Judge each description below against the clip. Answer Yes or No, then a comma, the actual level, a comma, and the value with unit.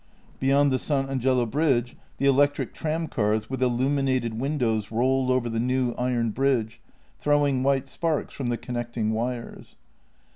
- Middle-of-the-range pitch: No, low, 130 Hz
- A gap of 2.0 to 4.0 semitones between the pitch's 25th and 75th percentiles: Yes, narrow, 2.6 semitones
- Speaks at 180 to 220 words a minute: No, average, 140 wpm